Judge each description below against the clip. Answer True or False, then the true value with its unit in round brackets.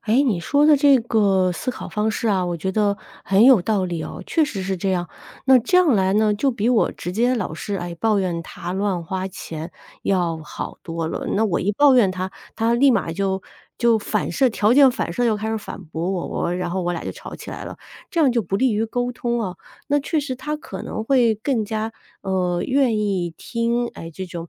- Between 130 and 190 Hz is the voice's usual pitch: False (210 Hz)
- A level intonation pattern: False (4.8 semitones)